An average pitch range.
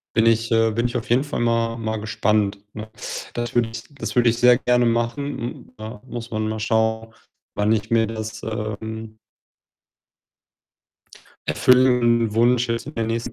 No: narrow, 1.4 semitones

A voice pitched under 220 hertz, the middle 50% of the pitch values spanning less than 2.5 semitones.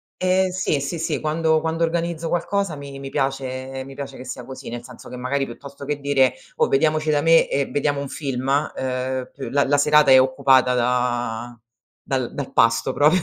No: medium, 140 Hz; average, 2.9 semitones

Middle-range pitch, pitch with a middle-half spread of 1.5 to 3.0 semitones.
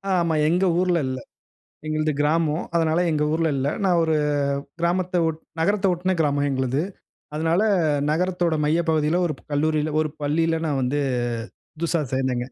Yes: medium, 160 Hz; narrow, 2.4 semitones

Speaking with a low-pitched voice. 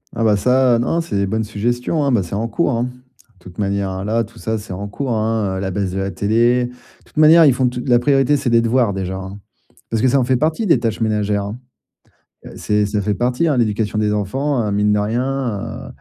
Yes: low, 115 Hz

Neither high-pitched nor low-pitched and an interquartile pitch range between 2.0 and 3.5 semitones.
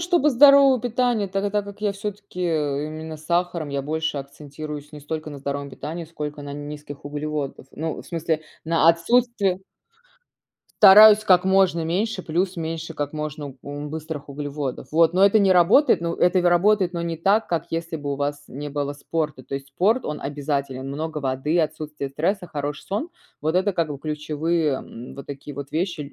No: medium, 160 Hz; average, 4.2 semitones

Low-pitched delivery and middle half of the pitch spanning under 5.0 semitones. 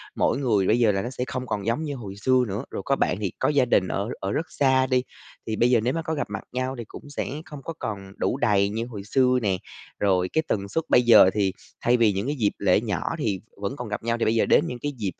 Yes: low, 115 Hz; average, 4.3 semitones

